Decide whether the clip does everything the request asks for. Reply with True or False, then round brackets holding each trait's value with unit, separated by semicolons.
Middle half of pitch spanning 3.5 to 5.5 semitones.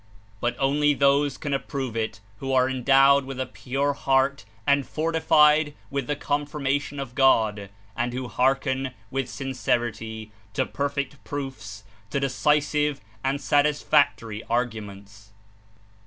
False (2.9 semitones)